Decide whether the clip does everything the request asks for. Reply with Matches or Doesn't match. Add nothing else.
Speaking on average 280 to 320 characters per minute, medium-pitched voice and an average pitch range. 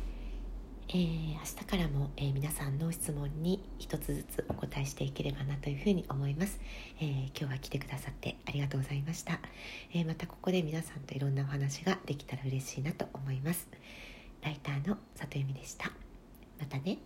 Doesn't match